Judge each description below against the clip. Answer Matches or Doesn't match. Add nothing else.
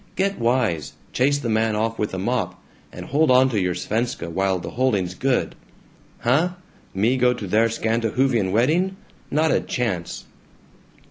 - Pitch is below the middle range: Matches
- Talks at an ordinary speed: Matches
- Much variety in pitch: Doesn't match